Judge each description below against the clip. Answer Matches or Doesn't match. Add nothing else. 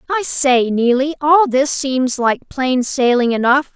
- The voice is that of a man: Doesn't match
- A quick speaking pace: Doesn't match